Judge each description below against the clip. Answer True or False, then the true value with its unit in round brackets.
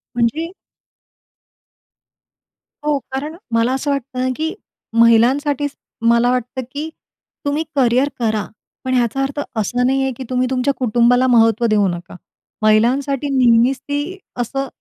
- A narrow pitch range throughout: False (3.1 semitones)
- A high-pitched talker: True (255 Hz)